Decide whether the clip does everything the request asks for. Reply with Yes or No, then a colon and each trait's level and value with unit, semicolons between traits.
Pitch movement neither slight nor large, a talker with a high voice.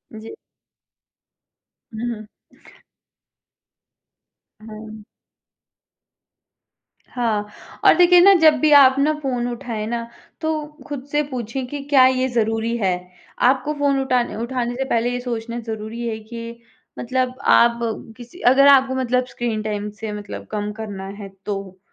Yes: average, 3.1 semitones; high, 240 Hz